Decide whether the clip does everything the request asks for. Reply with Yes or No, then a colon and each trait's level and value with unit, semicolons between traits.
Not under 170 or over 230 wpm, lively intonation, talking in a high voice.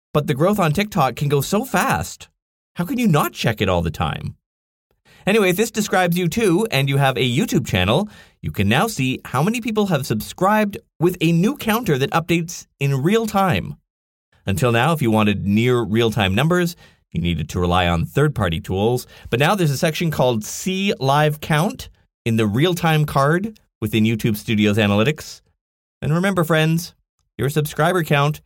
No: average, 190 wpm; wide, 8.1 semitones; medium, 145 Hz